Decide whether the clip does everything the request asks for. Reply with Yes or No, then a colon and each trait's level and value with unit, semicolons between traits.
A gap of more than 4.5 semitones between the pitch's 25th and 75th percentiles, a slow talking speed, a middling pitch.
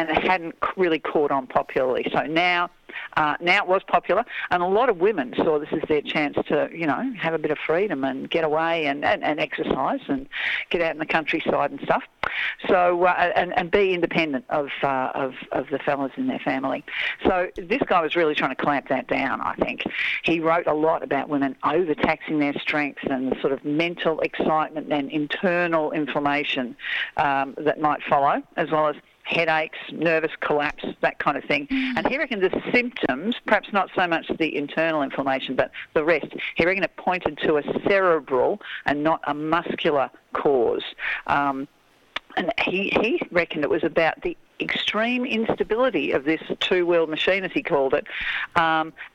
No: wide, 5.5 semitones; average, 185 wpm; medium, 165 Hz